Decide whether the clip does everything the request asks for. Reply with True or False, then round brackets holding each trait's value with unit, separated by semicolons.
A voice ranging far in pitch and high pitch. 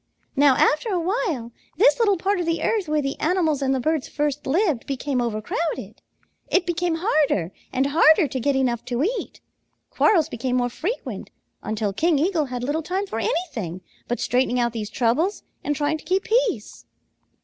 True (5.9 semitones; 295 Hz)